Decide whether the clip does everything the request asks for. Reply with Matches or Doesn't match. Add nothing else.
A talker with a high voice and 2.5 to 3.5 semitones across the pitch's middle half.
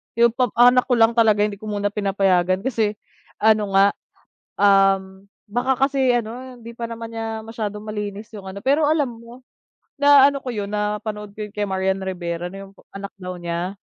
Matches